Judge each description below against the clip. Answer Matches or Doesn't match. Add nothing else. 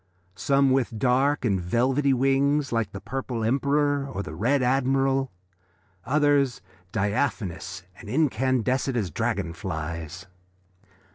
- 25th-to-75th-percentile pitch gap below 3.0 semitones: Doesn't match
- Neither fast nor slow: Doesn't match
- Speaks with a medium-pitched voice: Doesn't match